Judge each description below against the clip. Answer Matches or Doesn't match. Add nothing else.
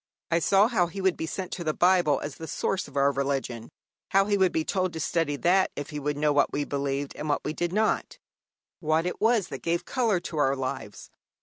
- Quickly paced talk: Matches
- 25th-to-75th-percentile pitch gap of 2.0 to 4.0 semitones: Doesn't match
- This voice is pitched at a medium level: Matches